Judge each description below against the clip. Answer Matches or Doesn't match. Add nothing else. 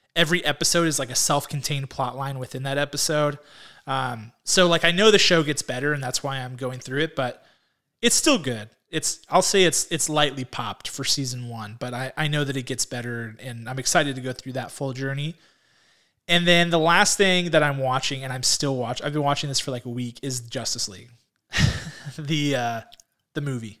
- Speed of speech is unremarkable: Doesn't match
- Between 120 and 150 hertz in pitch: Matches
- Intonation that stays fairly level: Doesn't match